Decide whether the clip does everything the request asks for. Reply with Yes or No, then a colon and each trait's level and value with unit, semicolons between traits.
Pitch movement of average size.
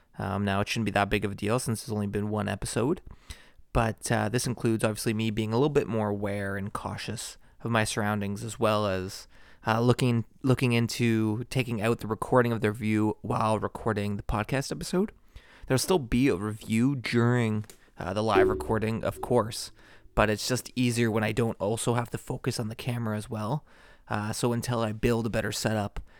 No: narrow, 2.3 semitones